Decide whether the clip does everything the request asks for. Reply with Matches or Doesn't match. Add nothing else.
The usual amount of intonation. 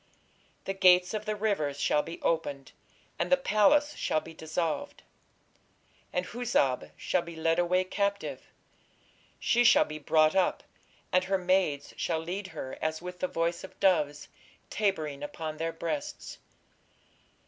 Matches